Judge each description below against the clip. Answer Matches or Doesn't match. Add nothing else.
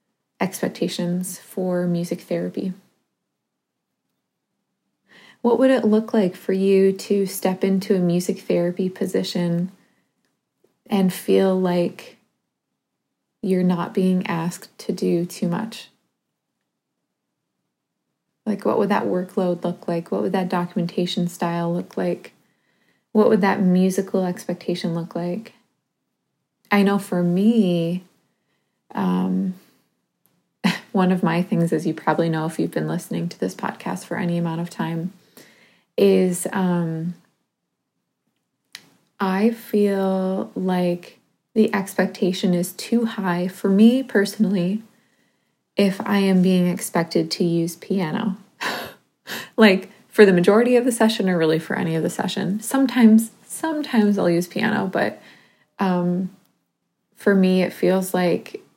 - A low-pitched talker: Doesn't match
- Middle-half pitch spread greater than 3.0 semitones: Doesn't match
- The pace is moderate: Doesn't match